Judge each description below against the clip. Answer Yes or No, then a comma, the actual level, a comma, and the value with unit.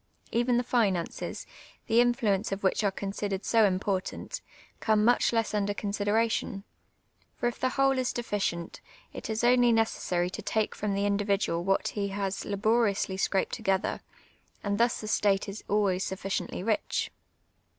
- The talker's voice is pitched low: No, high, 205 Hz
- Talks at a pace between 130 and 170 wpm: Yes, average, 155 wpm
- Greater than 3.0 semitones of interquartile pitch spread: No, average, 2.7 semitones